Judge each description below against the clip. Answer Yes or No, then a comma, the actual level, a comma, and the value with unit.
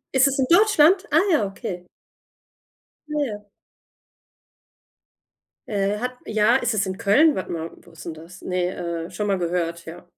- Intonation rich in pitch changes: Yes, wide, 6.4 semitones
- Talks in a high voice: Yes, high, 200 Hz